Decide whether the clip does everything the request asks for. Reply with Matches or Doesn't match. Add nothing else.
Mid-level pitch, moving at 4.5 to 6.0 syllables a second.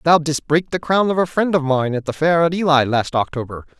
Matches